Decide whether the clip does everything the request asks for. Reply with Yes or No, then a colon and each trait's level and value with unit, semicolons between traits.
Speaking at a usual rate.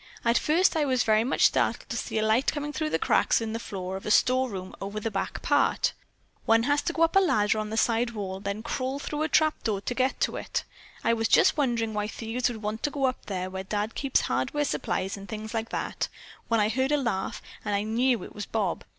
No: fast, 245 wpm